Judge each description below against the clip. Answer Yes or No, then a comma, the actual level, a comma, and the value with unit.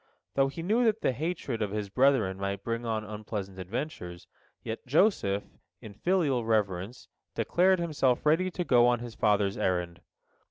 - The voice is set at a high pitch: No, low, 115 Hz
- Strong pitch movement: Yes, wide, 7.1 semitones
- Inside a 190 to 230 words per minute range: No, average, 160 wpm